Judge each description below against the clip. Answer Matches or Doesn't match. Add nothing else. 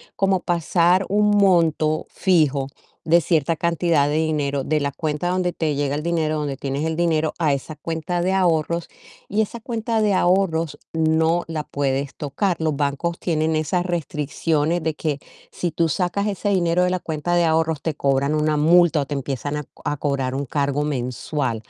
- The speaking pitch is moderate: Matches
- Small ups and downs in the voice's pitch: Doesn't match